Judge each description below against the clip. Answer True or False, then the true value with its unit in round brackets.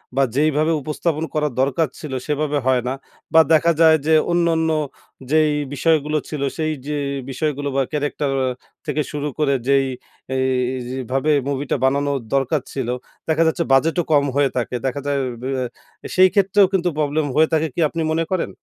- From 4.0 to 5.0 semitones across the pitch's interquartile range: False (2.7 semitones)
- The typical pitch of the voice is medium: True (150 Hz)